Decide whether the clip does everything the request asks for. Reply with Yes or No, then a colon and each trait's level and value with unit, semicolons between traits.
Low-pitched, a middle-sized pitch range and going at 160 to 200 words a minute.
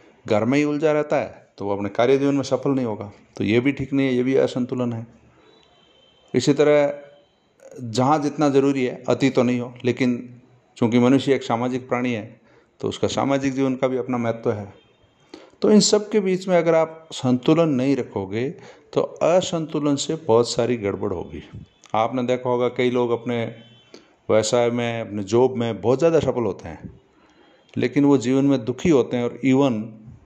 Yes: low, 125 Hz; average, 3.0 semitones; fast, 190 wpm